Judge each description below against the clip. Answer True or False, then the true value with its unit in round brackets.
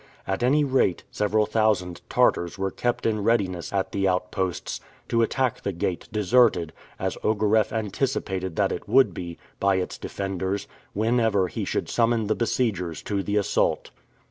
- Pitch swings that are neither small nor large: True (3.3 semitones)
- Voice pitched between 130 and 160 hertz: False (100 Hz)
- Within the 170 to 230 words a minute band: False (155 wpm)